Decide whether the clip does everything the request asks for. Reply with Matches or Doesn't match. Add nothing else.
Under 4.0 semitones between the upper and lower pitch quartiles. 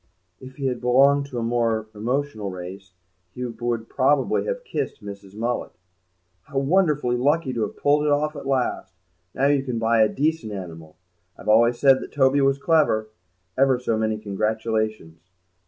Doesn't match